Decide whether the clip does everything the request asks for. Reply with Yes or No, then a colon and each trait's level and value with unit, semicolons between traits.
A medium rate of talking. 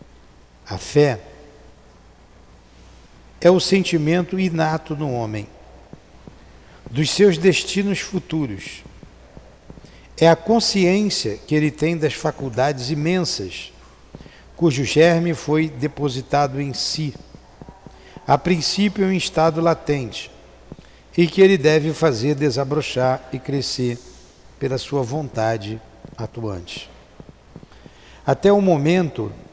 No: slow, 95 wpm